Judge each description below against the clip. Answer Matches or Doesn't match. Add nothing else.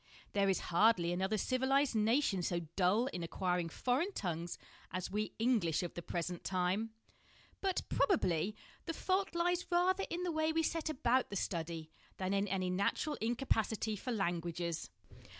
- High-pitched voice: Matches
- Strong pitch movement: Matches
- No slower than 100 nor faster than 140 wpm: Doesn't match